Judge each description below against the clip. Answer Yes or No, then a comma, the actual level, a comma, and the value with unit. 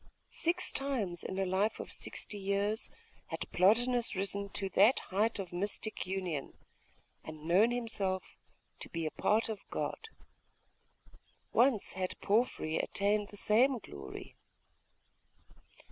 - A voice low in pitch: No, high, 200 Hz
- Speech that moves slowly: Yes, slow, 125 wpm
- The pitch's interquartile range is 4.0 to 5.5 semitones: No, average, 3.2 semitones